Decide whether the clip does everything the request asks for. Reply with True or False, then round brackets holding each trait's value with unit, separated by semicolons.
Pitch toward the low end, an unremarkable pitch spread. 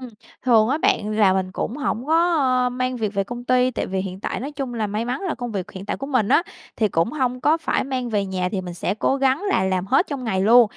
False (240 Hz; 4.8 semitones)